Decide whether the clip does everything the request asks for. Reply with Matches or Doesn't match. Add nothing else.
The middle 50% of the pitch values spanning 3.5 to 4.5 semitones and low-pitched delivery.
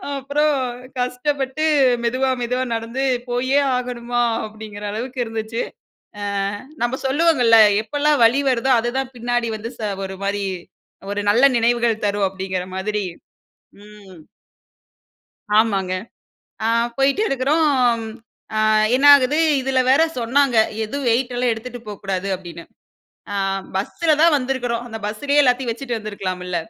Doesn't match